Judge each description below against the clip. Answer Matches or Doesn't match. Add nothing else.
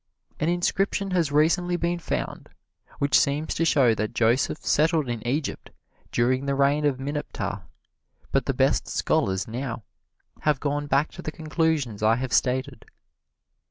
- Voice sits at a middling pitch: Matches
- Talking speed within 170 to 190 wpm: Doesn't match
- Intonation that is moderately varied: Matches